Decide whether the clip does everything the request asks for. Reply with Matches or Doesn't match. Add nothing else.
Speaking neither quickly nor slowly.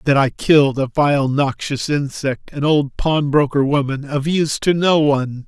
Matches